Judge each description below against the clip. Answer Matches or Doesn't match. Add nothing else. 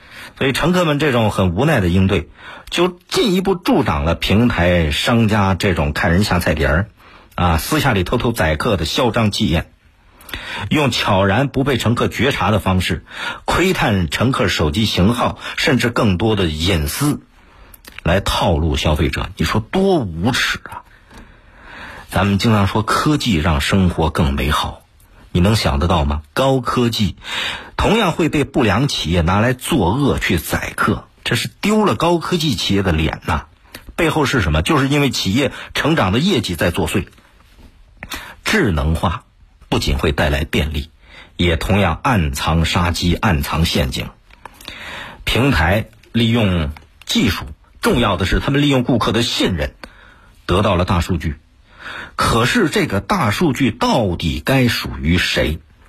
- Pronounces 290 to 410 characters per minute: Doesn't match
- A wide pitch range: Matches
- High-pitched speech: Doesn't match